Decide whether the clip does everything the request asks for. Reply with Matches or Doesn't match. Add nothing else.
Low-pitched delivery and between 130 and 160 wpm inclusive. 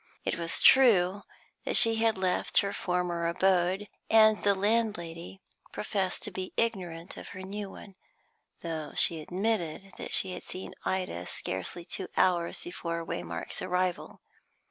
Doesn't match